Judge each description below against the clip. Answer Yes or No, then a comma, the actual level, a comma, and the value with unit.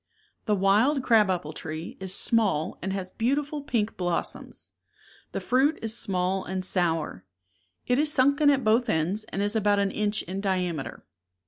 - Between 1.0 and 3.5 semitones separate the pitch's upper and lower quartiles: No, average, 4.6 semitones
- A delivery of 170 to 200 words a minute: Yes, average, 180 wpm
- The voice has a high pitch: Yes, high, 205 Hz